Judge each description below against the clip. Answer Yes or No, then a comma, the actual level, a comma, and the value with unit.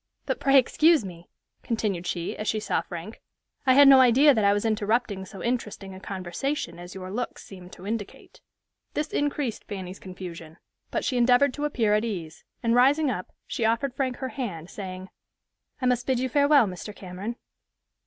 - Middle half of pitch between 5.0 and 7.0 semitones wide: Yes, wide, 5.6 semitones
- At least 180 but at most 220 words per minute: Yes, average, 185 wpm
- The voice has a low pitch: No, high, 220 Hz